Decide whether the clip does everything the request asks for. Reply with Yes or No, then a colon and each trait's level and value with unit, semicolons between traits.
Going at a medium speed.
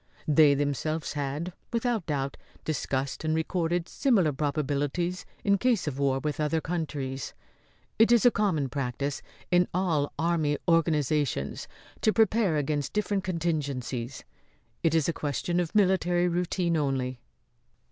No: slow, 130 wpm